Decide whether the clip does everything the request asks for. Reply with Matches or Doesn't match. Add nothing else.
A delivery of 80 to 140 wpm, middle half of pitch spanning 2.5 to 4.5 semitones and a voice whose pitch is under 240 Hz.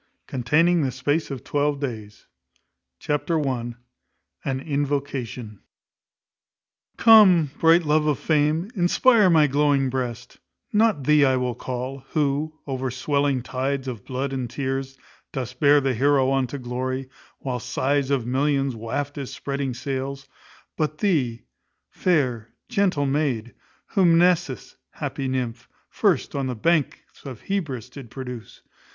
Matches